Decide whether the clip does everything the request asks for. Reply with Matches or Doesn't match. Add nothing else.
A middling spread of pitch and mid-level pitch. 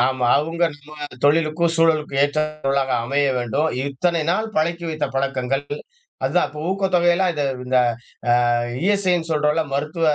Matches